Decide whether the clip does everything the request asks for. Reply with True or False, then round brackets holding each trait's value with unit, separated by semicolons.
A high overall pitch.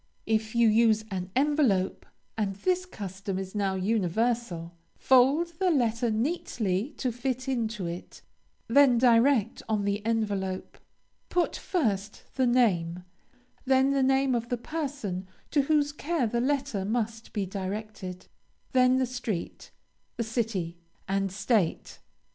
True (225 Hz)